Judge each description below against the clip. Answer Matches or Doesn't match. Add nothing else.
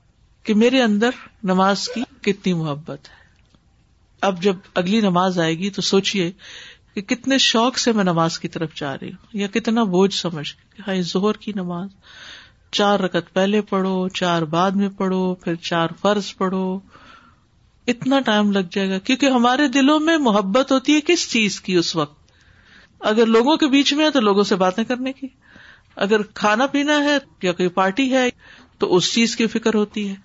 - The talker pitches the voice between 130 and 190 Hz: Doesn't match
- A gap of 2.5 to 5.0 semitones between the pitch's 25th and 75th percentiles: Matches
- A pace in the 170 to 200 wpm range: Matches